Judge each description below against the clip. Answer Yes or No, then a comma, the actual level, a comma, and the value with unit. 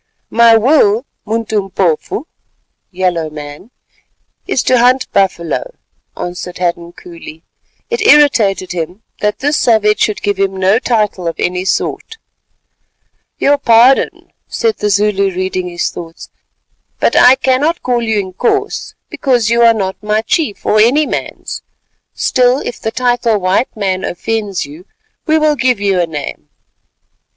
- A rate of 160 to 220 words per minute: No, average, 140 wpm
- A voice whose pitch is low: No, high, 210 Hz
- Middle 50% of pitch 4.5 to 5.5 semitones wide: Yes, average, 5.1 semitones